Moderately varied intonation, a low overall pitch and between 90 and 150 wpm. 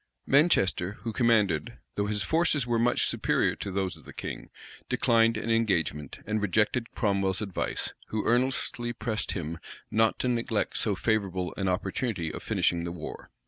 No: average, 3.8 semitones; low, 105 Hz; average, 160 wpm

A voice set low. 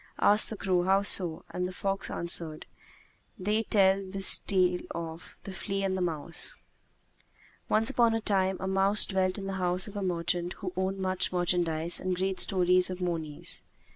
No: medium, 185 Hz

